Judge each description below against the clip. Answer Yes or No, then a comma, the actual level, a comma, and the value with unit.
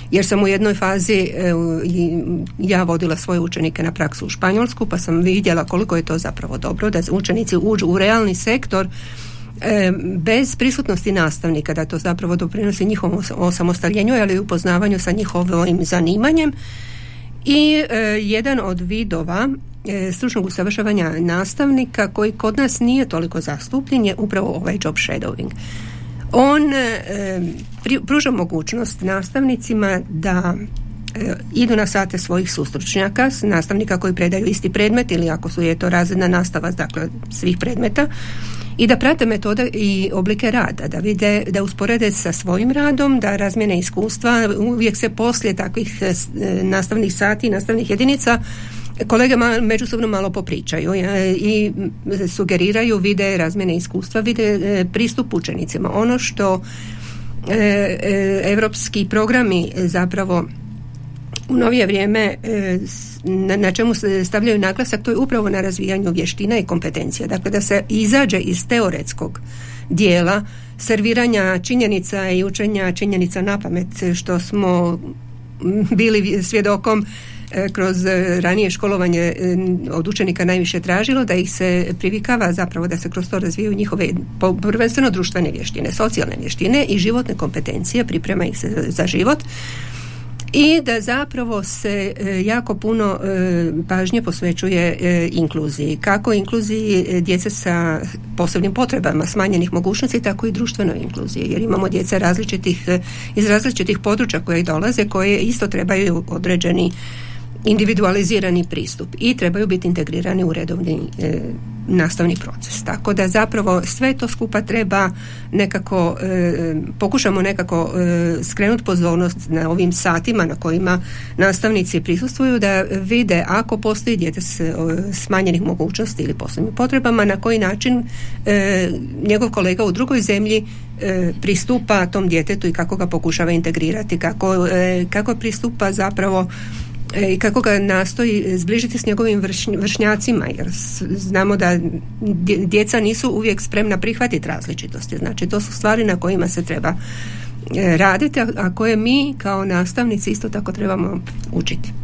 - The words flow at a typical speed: Yes, average, 135 wpm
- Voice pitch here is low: No, high, 190 Hz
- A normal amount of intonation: Yes, average, 3.8 semitones